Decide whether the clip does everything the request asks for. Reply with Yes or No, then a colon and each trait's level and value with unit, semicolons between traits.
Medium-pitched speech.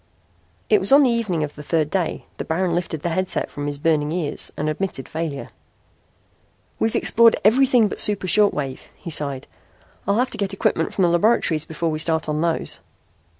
Yes: medium, 170 Hz